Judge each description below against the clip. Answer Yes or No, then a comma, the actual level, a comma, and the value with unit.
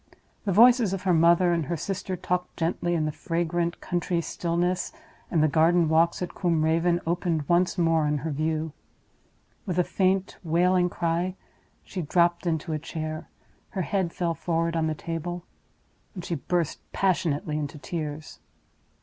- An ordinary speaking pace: Yes, average, 160 wpm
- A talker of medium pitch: Yes, medium, 170 Hz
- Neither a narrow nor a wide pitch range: No, narrow, 1.9 semitones